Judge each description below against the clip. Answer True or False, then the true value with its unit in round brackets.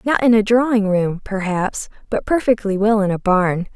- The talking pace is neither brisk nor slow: True (190 wpm)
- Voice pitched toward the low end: False (210 Hz)